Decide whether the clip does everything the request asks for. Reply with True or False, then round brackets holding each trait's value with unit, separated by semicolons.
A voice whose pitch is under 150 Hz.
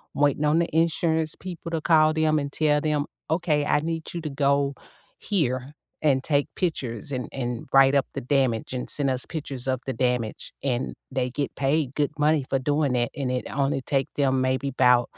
True (140 Hz)